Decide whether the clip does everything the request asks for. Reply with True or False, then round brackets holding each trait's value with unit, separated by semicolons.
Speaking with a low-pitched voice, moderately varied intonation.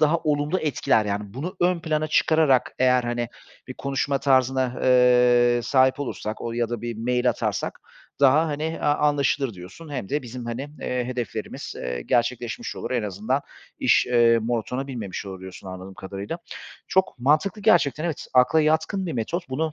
True (130 Hz; 4.2 semitones)